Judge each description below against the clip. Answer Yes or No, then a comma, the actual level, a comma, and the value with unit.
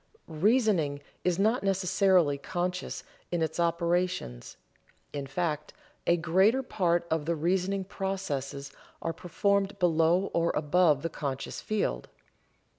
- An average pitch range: Yes, average, 3.4 semitones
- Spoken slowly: Yes, slow, 115 wpm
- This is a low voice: No, medium, 175 Hz